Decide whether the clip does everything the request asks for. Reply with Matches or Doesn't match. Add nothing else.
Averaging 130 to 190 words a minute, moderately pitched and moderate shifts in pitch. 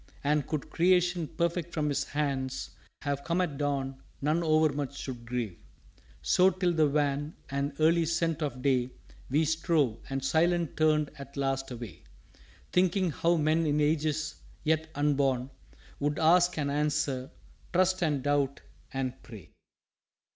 Matches